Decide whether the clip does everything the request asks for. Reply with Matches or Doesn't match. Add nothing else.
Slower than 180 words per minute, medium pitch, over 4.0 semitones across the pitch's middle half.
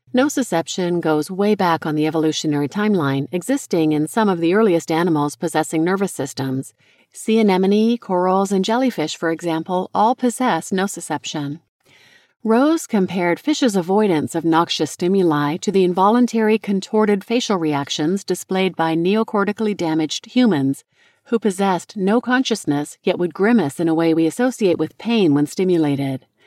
Matches